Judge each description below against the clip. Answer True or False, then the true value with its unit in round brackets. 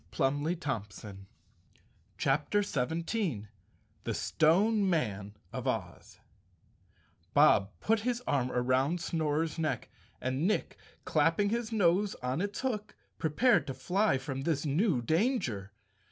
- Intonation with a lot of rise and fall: True (7.6 semitones)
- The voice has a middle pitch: True (160 Hz)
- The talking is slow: True (115 wpm)